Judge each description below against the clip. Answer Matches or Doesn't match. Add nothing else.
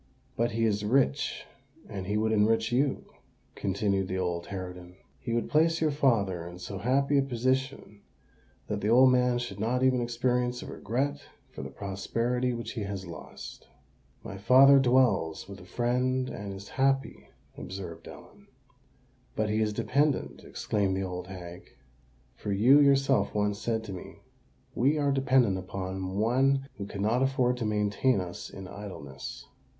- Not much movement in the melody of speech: Doesn't match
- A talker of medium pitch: Doesn't match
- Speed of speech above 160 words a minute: Doesn't match